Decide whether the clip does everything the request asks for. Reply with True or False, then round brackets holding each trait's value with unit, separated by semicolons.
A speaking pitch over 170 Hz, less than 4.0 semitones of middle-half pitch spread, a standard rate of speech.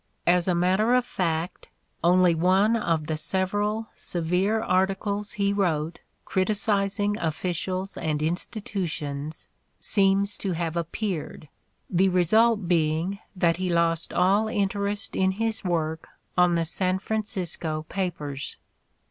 False (185 Hz; 3.2 semitones; 125 wpm)